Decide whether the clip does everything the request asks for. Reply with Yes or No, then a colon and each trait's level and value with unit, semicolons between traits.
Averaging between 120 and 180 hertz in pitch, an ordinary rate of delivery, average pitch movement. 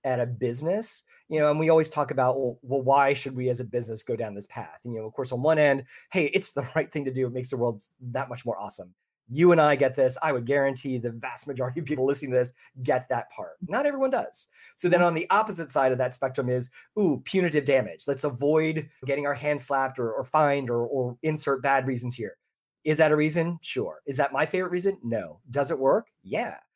No: medium, 140 Hz; fast, 245 wpm; average, 3.4 semitones